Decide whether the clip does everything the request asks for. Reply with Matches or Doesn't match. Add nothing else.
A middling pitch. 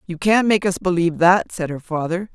Matches